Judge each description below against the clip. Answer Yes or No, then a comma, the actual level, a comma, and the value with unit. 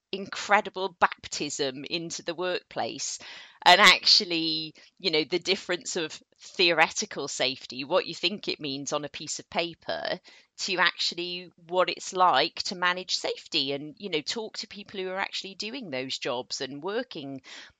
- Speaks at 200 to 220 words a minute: No, average, 155 wpm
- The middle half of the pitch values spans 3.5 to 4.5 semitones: Yes, average, 3.9 semitones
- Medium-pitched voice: Yes, medium, 180 Hz